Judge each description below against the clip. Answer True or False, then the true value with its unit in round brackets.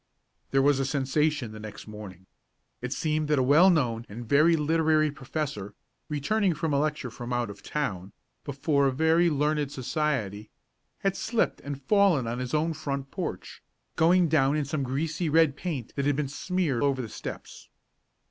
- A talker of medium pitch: True (145 Hz)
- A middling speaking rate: True (175 wpm)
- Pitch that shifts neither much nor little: True (3.5 semitones)